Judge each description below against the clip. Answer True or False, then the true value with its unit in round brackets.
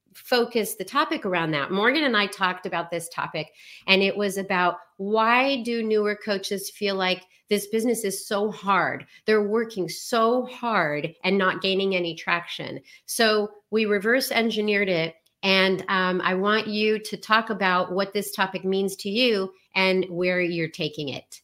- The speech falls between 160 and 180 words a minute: True (170 wpm)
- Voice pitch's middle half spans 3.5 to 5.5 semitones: False (2.9 semitones)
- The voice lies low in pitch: False (195 Hz)